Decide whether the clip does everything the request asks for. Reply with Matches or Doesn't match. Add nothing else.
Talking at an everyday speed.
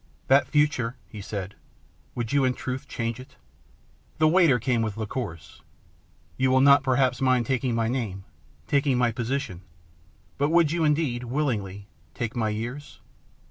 Matches